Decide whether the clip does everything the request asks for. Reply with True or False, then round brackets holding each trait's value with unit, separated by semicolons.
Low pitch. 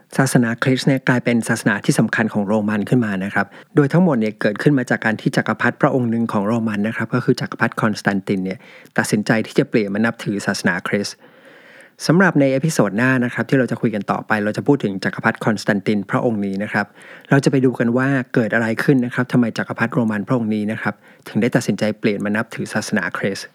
True (120 Hz)